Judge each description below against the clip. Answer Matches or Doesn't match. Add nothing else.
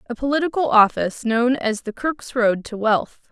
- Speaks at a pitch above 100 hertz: Matches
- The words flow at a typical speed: Matches